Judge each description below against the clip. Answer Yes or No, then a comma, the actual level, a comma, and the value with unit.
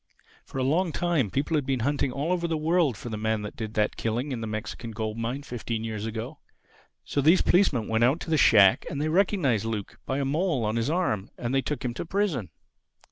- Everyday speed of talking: No, fast, 235 wpm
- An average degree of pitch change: No, wide, 5.8 semitones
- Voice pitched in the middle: No, low, 130 Hz